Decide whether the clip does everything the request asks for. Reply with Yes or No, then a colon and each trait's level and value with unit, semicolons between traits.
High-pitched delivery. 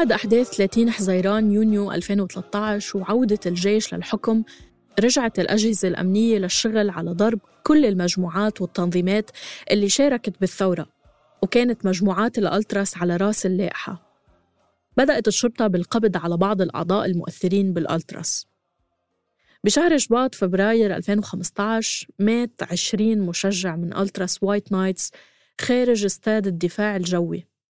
Yes: high, 200 Hz